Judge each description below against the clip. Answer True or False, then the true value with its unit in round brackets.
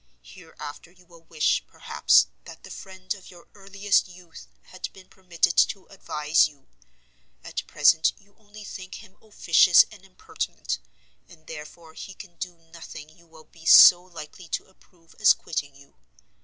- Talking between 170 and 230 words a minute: False (155 wpm)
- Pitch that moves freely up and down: False (3.0 semitones)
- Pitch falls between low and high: True (175 Hz)